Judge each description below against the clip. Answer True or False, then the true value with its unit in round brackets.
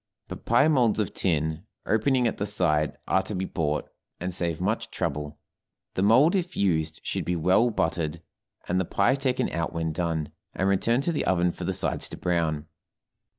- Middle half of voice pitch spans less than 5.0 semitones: False (5.6 semitones)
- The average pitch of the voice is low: True (90 Hz)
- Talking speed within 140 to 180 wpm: False (190 wpm)